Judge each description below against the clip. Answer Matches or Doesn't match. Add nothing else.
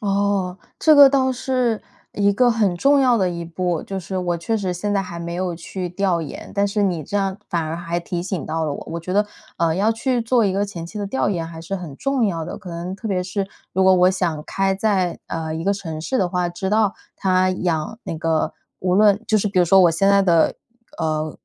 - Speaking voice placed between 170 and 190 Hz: Matches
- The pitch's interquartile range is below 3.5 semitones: Matches